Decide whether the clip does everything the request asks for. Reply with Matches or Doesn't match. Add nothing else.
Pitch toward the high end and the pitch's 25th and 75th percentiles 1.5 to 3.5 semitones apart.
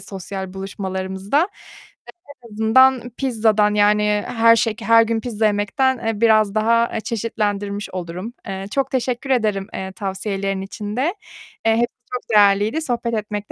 Matches